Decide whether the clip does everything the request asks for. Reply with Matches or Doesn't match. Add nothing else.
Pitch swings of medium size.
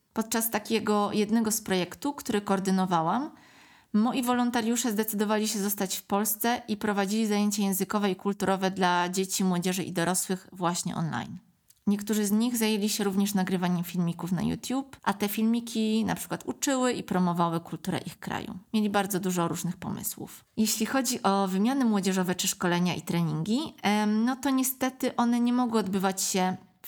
Matches